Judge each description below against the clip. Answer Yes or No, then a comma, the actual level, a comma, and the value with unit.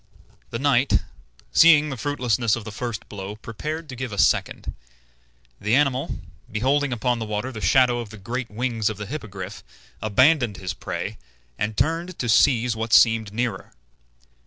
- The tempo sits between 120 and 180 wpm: Yes, average, 160 wpm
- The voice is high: No, low, 120 Hz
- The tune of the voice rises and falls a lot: No, average, 3.6 semitones